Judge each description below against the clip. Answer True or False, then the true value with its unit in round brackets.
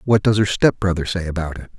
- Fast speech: True (235 wpm)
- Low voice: True (95 Hz)